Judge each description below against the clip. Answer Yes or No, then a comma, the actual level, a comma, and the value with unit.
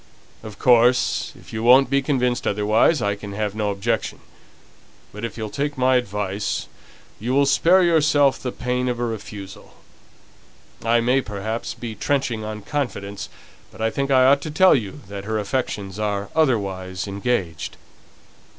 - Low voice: Yes, low, 115 Hz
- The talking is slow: No, average, 160 wpm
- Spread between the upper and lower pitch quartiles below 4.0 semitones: No, average, 4.3 semitones